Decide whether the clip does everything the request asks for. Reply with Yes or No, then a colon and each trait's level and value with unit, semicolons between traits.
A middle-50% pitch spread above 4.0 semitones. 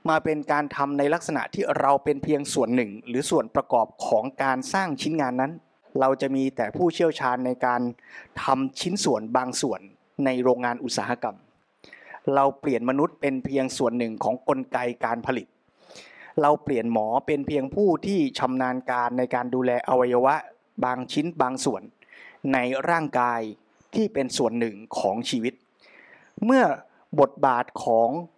No: average, 3.0 semitones